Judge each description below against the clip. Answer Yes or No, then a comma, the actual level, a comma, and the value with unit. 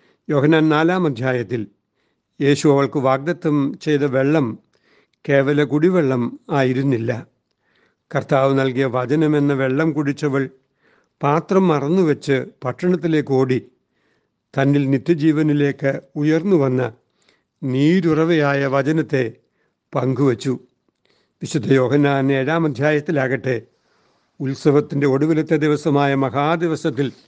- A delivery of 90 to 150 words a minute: No, average, 80 wpm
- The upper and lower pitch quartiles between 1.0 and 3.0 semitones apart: Yes, narrow, 2.6 semitones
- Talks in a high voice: No, medium, 140 Hz